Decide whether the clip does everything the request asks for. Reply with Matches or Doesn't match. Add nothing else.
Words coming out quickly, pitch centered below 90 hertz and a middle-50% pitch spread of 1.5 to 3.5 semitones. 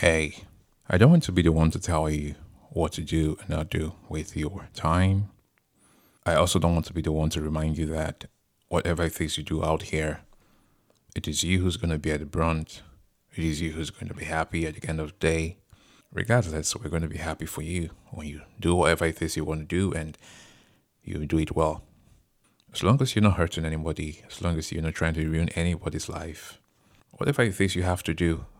Matches